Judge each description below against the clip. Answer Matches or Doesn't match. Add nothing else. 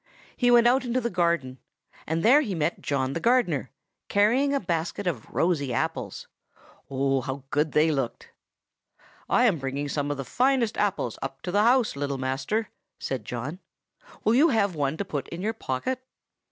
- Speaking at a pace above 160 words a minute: Matches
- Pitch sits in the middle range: Matches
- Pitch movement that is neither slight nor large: Doesn't match